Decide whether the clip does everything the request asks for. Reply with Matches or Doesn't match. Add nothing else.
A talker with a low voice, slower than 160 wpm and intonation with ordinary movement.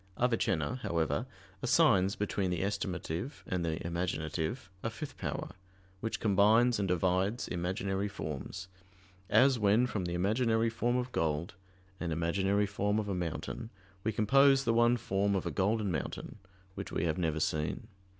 Matches